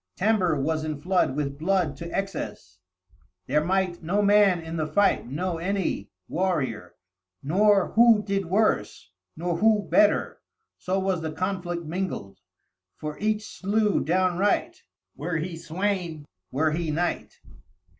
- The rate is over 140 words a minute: No, slow, 135 wpm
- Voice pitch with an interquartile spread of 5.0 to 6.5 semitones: No, average, 3.9 semitones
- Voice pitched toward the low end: No, medium, 175 Hz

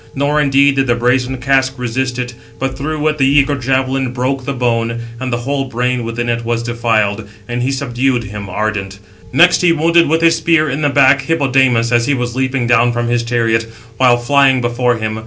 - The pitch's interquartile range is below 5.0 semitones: Yes, narrow, 2.5 semitones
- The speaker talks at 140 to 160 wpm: No, average, 200 wpm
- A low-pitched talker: Yes, low, 125 Hz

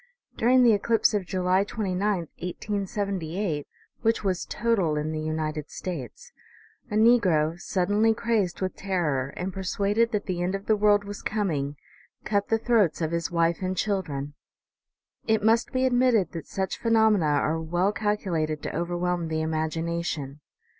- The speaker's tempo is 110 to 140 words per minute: No, average, 155 wpm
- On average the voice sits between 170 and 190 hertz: Yes, medium, 185 Hz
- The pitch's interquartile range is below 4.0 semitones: No, average, 4.5 semitones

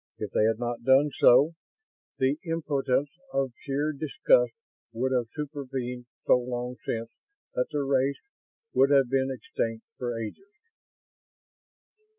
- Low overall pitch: Yes, low, 130 Hz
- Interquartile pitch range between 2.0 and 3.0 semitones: Yes, average, 2.7 semitones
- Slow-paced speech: Yes, slow, 130 wpm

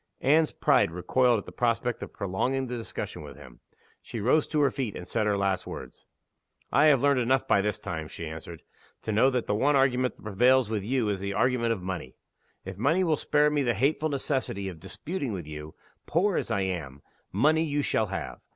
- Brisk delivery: Yes, fast, 215 wpm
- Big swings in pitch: Yes, wide, 6.1 semitones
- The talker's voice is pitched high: No, low, 115 Hz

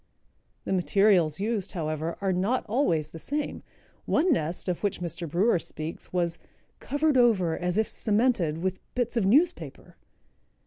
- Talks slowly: No, average, 145 wpm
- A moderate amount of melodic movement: No, wide, 5.7 semitones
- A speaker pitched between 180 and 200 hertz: Yes, high, 190 Hz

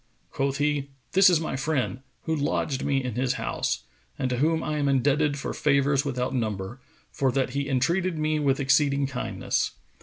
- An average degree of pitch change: No, narrow, 2.3 semitones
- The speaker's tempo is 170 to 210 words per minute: Yes, average, 180 wpm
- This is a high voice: No, medium, 140 Hz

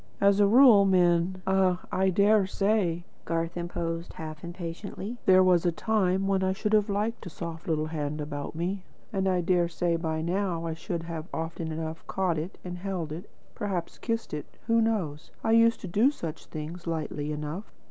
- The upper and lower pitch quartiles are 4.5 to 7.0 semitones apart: No, average, 3.2 semitones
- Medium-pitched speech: Yes, medium, 175 Hz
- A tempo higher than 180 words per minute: Yes, average, 190 wpm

